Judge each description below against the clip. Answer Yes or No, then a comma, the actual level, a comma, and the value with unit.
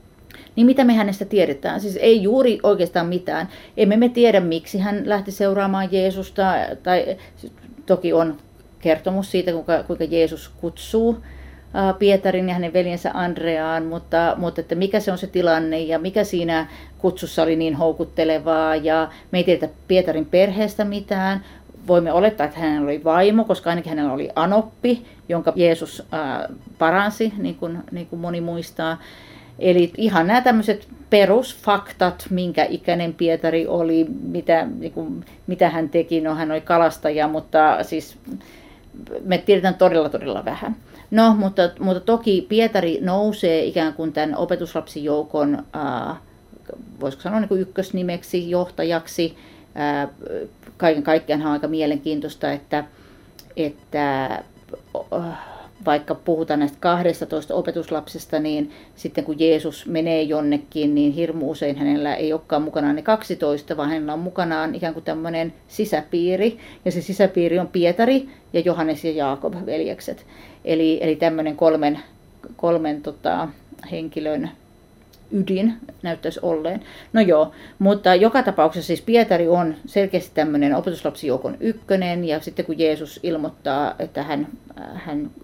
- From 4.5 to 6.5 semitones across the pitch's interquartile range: No, average, 3.3 semitones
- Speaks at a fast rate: No, average, 135 wpm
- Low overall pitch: No, medium, 170 Hz